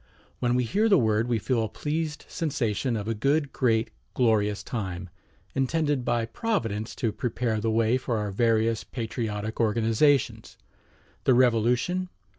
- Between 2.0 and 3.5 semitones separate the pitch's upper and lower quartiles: Yes, average, 3.1 semitones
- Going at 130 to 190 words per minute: Yes, average, 145 wpm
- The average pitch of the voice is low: Yes, low, 115 Hz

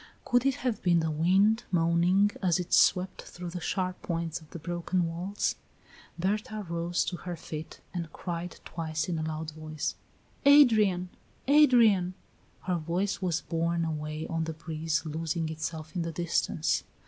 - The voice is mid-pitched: Yes, medium, 170 Hz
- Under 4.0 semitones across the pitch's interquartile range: Yes, narrow, 2.6 semitones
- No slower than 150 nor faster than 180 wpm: Yes, average, 160 wpm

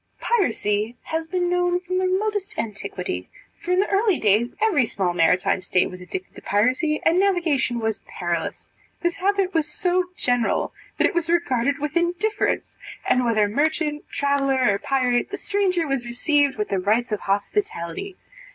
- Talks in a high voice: Yes, very high, 285 Hz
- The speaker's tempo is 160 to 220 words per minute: Yes, average, 165 wpm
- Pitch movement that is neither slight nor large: No, wide, 8.7 semitones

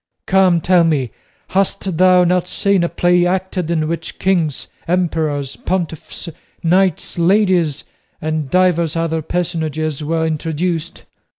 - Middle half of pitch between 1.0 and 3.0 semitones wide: Yes, narrow, 2.5 semitones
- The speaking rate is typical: No, slow, 120 wpm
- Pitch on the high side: No, medium, 170 Hz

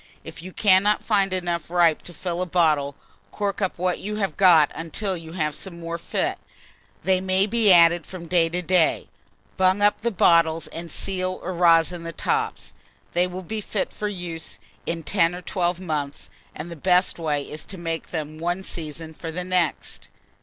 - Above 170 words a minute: Yes, average, 190 wpm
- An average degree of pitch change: No, narrow, 2.2 semitones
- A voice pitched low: No, medium, 175 Hz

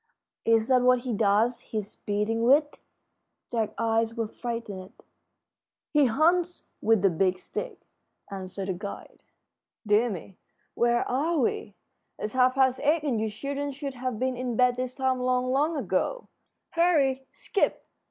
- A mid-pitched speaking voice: No, high, 245 Hz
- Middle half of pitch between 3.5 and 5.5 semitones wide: Yes, average, 3.8 semitones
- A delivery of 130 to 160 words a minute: Yes, average, 150 wpm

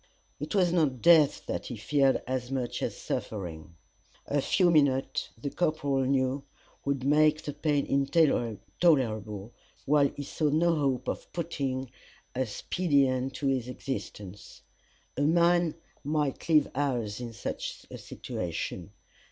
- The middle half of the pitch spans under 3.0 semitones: No, average, 3.3 semitones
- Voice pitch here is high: No, medium, 140 Hz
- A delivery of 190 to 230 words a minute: No, average, 140 wpm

